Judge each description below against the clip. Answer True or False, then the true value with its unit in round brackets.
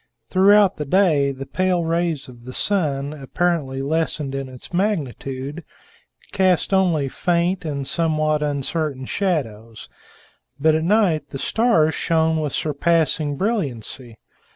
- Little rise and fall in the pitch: False (4.4 semitones)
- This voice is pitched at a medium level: True (155 Hz)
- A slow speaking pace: True (125 wpm)